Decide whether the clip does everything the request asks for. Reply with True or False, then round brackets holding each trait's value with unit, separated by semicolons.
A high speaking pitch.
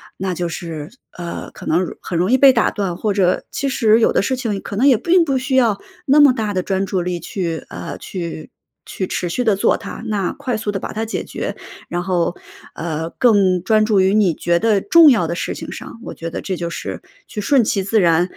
True (195 Hz)